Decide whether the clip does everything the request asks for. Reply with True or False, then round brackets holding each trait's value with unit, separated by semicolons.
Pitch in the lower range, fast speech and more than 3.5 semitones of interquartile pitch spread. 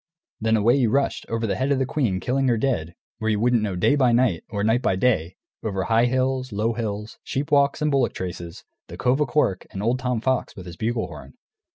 True (115 Hz; 235 wpm; 4.0 semitones)